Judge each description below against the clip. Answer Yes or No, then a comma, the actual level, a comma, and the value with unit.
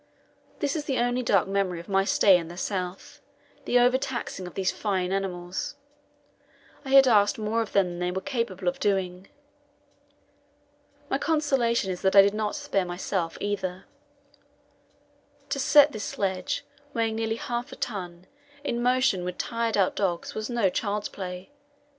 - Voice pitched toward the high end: Yes, high, 200 Hz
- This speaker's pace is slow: No, average, 165 wpm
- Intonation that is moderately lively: Yes, average, 4.5 semitones